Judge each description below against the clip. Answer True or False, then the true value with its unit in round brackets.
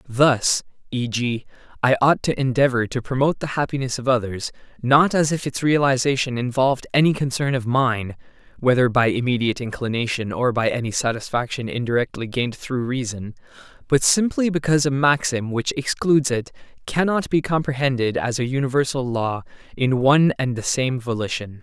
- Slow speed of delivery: False (155 wpm)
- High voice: False (130 Hz)